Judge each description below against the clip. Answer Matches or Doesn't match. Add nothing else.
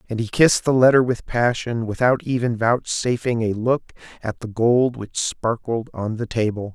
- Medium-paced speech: Matches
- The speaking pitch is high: Doesn't match